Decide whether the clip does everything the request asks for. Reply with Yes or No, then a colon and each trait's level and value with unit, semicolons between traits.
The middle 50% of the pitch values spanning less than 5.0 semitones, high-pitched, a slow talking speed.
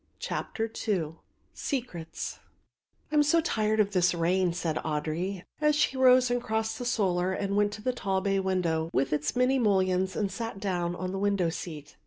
No: average, 4.3 semitones; high, 195 Hz; average, 185 wpm